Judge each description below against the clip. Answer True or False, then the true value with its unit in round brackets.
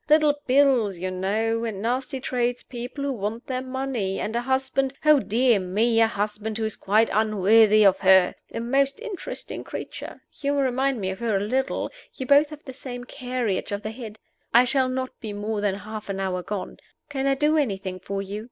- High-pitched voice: True (230 Hz)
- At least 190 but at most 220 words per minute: True (200 wpm)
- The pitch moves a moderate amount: True (4.3 semitones)